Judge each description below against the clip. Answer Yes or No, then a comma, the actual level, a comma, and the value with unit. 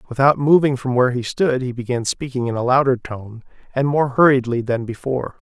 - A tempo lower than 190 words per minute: No, average, 200 wpm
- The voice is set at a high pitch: No, low, 130 Hz